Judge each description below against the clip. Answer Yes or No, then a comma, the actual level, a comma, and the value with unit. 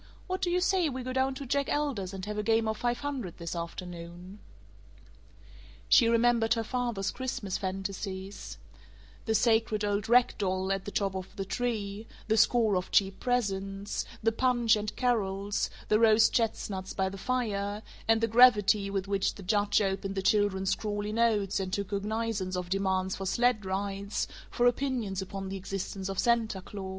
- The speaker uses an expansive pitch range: No, average, 3.2 semitones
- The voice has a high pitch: Yes, high, 205 Hz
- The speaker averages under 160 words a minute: No, average, 175 wpm